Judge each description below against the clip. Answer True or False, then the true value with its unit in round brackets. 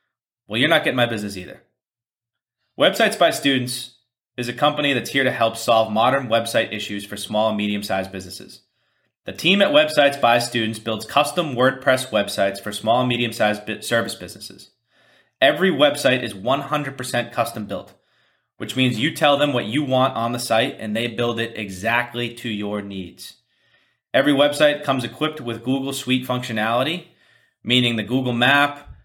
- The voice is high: False (120 Hz)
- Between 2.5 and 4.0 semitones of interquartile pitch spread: True (3.4 semitones)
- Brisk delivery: False (165 wpm)